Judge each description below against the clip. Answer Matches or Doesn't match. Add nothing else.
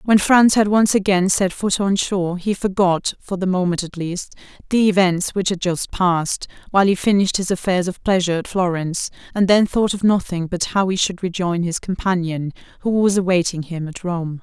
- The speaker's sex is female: Matches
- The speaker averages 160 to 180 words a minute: Doesn't match